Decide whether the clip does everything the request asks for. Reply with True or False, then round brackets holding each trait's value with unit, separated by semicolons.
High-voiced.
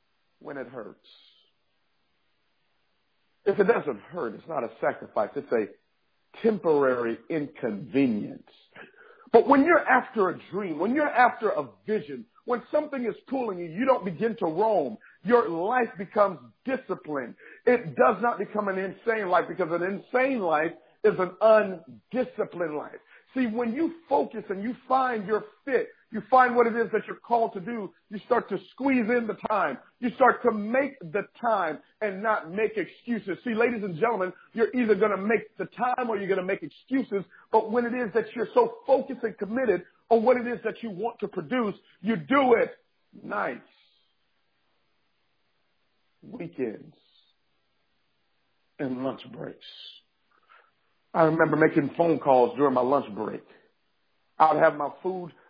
True (220 Hz)